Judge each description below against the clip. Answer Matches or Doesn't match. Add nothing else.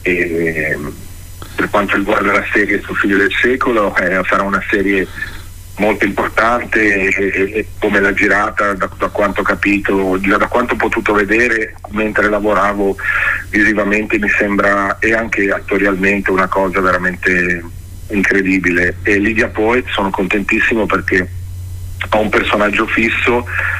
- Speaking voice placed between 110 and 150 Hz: Doesn't match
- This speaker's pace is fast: Doesn't match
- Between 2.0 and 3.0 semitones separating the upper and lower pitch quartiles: Matches